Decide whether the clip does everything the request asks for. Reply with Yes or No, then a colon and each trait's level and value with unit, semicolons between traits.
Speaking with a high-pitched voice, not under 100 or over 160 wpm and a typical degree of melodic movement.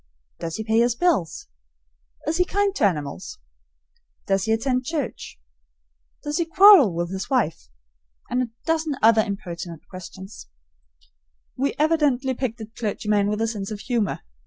No: high, 225 Hz; average, 150 wpm; wide, 6.6 semitones